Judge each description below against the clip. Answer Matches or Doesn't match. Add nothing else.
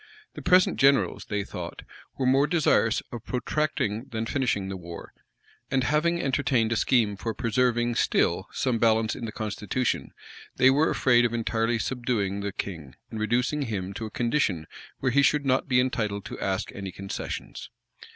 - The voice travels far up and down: Doesn't match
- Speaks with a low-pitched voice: Matches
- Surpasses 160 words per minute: Matches